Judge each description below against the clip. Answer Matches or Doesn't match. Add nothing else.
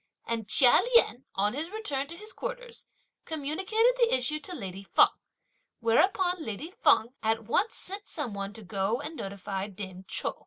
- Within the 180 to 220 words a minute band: Doesn't match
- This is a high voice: Matches